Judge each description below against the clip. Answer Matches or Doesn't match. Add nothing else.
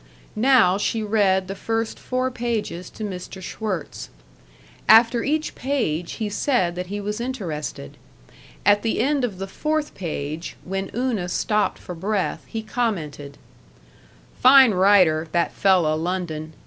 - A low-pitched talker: Doesn't match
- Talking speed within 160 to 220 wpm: Doesn't match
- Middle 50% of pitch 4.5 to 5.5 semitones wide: Matches